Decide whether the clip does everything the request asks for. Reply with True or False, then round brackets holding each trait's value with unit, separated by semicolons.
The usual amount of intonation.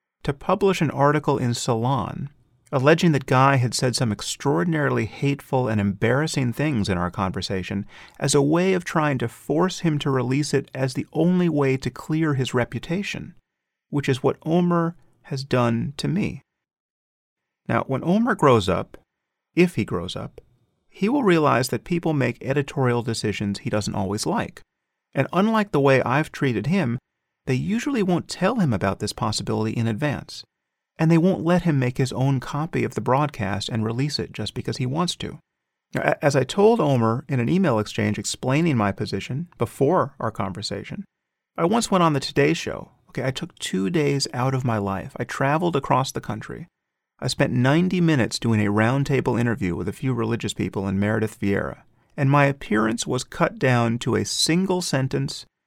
False (5.7 semitones)